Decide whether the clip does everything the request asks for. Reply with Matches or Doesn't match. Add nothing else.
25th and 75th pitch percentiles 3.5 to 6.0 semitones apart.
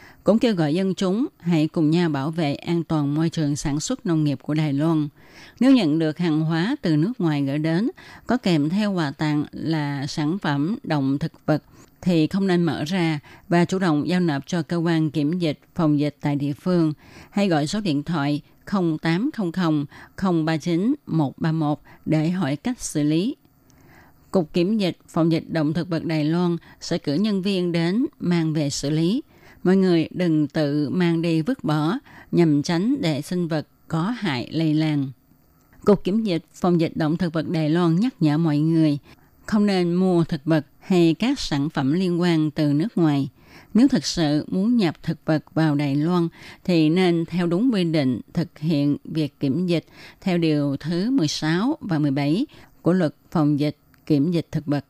Doesn't match